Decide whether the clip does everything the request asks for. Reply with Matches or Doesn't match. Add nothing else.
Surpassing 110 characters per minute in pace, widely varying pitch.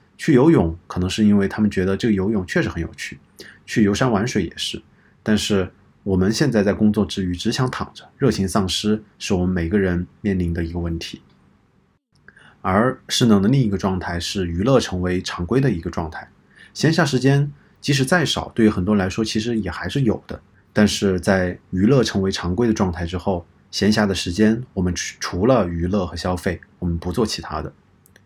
Doesn't match